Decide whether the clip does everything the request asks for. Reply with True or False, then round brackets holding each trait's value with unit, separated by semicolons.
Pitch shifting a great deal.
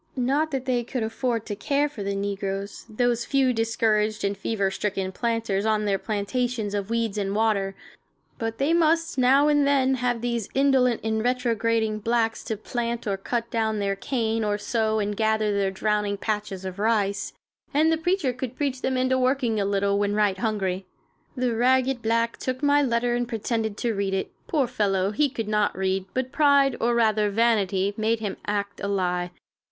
False (3.7 semitones)